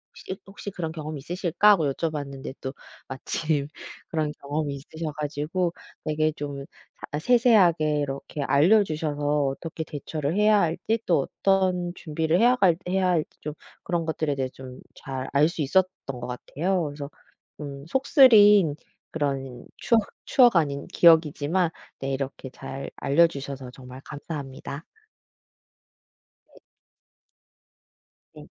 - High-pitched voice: No, medium, 155 Hz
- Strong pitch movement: No, average, 4.0 semitones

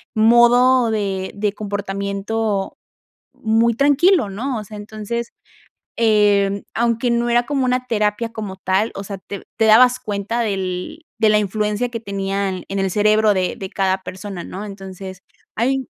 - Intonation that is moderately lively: Yes, average, 3.1 semitones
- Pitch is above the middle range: Yes, high, 210 Hz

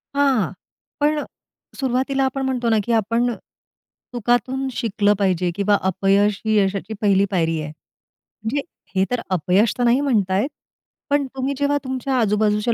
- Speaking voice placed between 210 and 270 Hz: Yes, high, 225 Hz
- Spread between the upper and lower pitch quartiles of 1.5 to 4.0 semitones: No, average, 4.8 semitones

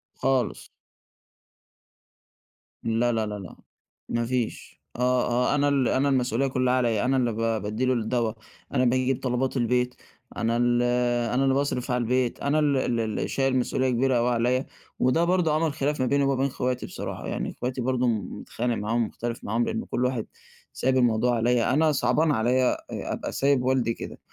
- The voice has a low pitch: Yes, low, 125 Hz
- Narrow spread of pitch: Yes, narrow, 1.9 semitones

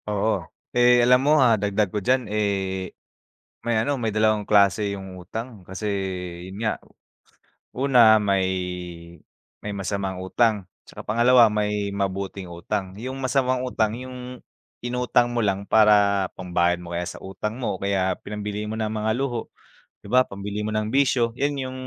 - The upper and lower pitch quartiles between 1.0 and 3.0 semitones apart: No, average, 3.6 semitones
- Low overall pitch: Yes, low, 105 Hz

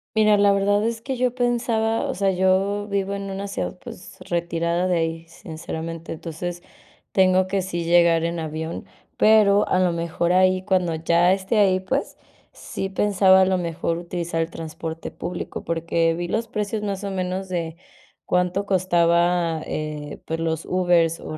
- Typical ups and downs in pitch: Yes, average, 3.0 semitones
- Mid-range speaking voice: Yes, medium, 180 Hz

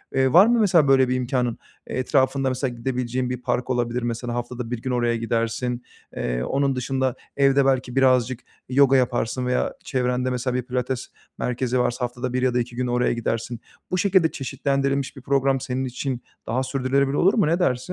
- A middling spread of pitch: No, narrow, 1.7 semitones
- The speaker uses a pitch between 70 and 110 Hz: No, low, 125 Hz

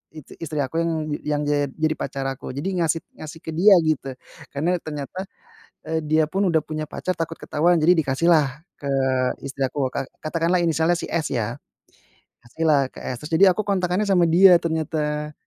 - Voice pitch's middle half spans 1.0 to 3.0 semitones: Yes, average, 2.7 semitones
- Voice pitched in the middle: Yes, medium, 160 Hz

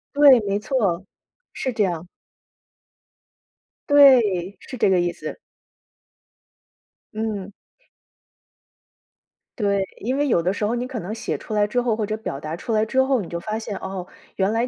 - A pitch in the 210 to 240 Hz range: Yes, high, 215 Hz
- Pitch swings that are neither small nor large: Yes, average, 4.2 semitones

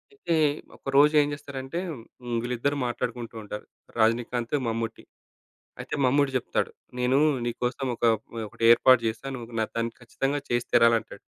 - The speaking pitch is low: Yes, low, 120 Hz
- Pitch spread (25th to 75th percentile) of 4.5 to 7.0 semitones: No, average, 2.7 semitones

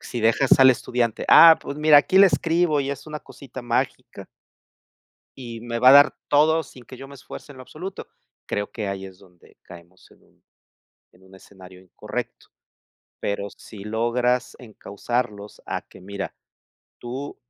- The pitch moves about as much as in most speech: No, wide, 5.7 semitones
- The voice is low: Yes, low, 120 Hz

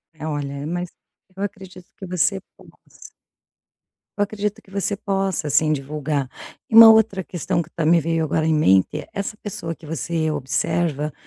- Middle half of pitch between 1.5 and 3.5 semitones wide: No, average, 4.3 semitones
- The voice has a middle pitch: Yes, medium, 165 Hz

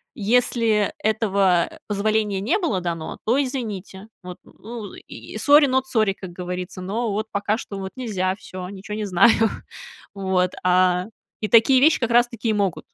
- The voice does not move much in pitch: No, average, 3.7 semitones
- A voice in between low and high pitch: No, high, 205 Hz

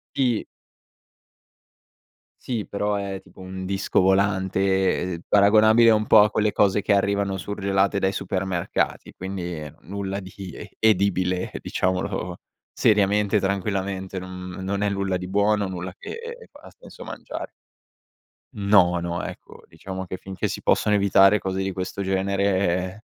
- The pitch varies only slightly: Yes, narrow, 1.5 semitones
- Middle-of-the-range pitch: No, very low, 95 Hz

